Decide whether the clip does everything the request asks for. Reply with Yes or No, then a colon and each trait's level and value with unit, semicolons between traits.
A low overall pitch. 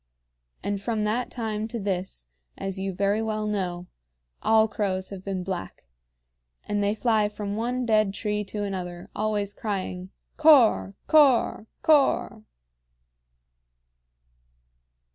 No: high, 210 Hz